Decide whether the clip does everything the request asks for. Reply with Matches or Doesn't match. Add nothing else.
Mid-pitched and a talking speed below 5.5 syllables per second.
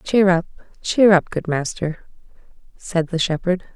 Matches